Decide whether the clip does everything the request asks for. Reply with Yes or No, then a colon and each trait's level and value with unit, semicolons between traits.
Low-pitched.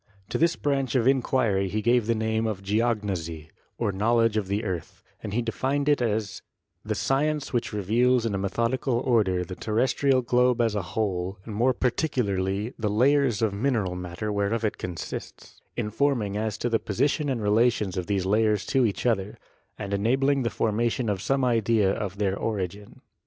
Yes: low, 110 Hz